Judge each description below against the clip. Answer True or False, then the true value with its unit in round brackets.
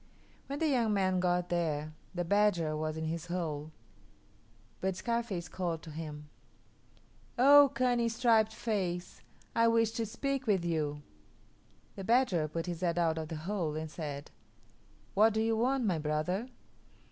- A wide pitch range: True (6.1 semitones)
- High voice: False (180 Hz)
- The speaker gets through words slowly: False (155 wpm)